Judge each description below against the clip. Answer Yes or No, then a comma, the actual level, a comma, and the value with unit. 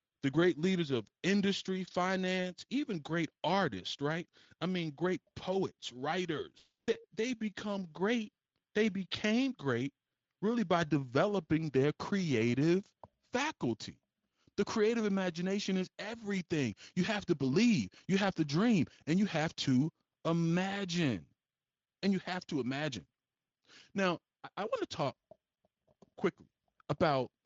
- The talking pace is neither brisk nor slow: No, slow, 130 wpm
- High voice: No, medium, 180 Hz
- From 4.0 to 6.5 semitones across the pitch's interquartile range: Yes, average, 4.6 semitones